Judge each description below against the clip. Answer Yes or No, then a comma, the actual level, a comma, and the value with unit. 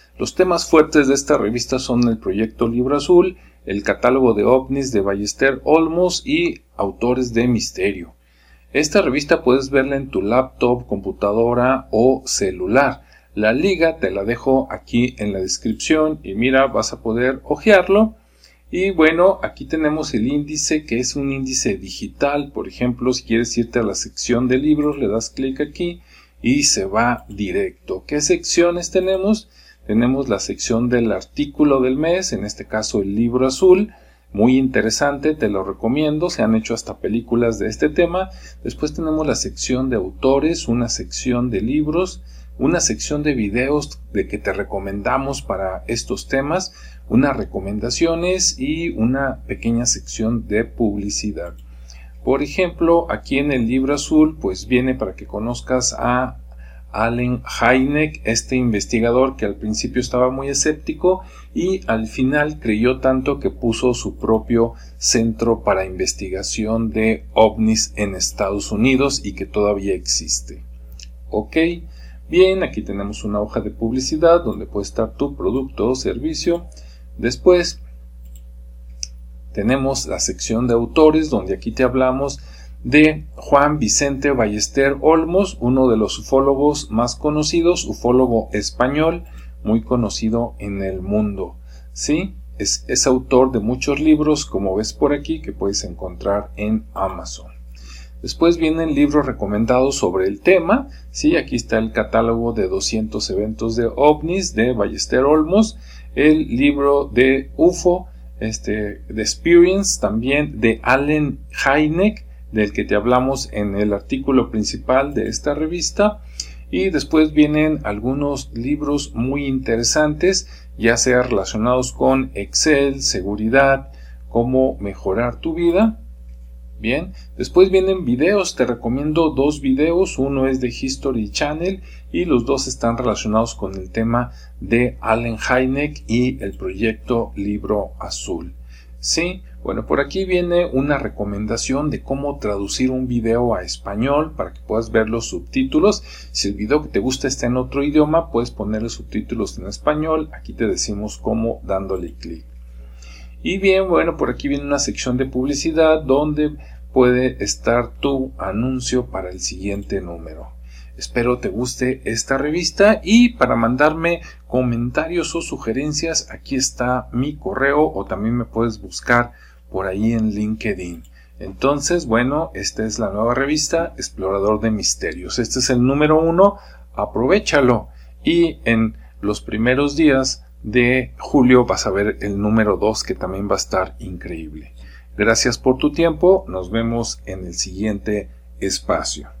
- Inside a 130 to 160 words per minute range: Yes, average, 145 wpm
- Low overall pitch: Yes, low, 120 Hz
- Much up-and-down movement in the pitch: Yes, wide, 6.1 semitones